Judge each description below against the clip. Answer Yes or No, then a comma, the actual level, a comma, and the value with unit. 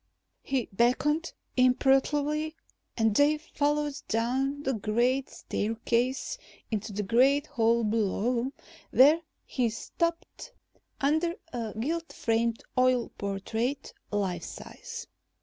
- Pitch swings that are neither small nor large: Yes, average, 4.4 semitones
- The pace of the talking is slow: Yes, slow, 100 wpm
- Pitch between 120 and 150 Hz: No, very high, 255 Hz